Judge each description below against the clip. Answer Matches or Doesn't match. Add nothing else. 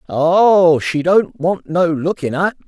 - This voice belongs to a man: Matches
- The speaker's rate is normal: Matches